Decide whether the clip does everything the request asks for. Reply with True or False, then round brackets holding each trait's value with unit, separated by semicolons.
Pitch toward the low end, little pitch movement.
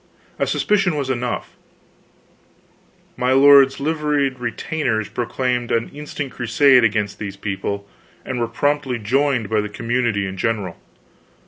False (125 Hz; 4.4 semitones)